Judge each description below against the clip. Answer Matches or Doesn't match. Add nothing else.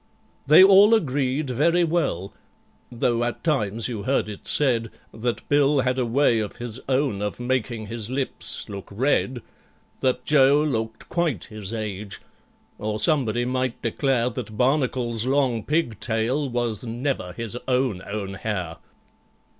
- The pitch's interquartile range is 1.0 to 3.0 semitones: Doesn't match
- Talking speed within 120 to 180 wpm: Matches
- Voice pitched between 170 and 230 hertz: Doesn't match